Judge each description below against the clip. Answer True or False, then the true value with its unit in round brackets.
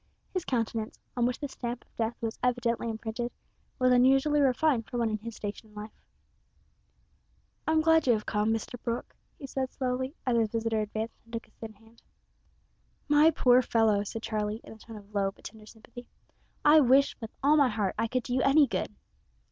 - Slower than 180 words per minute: False (200 wpm)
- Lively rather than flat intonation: False (2.8 semitones)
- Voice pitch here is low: False (235 Hz)